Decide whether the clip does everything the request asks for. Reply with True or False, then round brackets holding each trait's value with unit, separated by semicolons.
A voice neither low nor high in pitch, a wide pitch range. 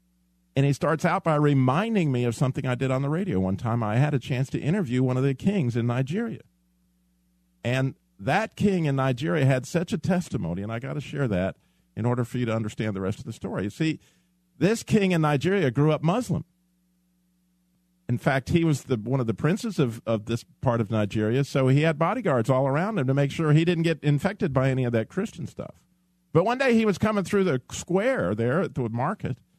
True (145 Hz; 6.6 semitones)